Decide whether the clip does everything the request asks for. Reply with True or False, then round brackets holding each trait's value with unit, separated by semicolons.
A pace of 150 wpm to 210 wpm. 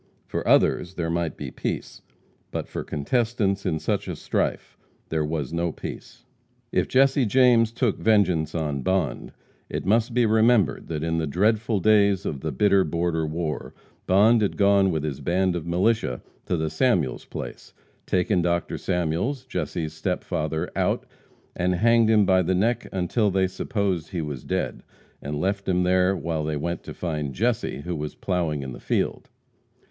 True (170 wpm)